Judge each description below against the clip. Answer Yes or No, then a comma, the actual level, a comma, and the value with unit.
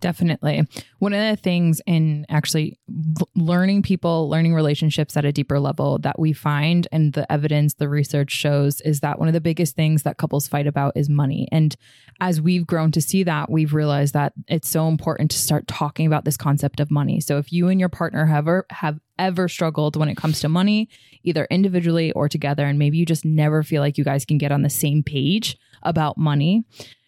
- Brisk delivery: Yes, fast, 210 wpm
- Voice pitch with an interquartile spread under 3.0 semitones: Yes, narrow, 2.5 semitones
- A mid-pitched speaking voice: Yes, medium, 155 Hz